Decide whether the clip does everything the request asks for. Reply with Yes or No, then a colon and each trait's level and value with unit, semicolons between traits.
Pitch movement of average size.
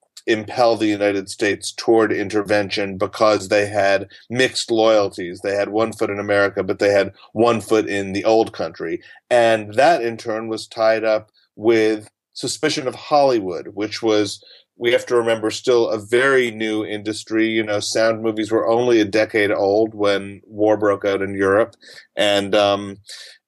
No: narrow, 1.9 semitones